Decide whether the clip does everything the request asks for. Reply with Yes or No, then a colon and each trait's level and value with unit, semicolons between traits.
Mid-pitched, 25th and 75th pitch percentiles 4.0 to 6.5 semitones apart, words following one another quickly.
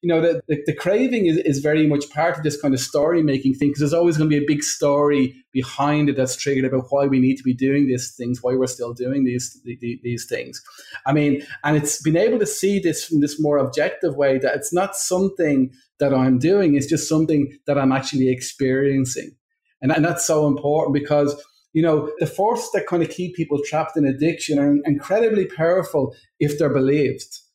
No: medium, 145 Hz; average, 3.3 semitones; fast, 220 wpm